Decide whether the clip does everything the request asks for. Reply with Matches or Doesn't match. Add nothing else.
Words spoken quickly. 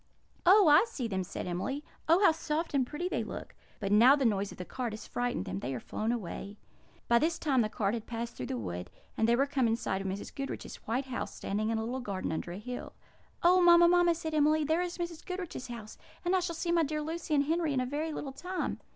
Matches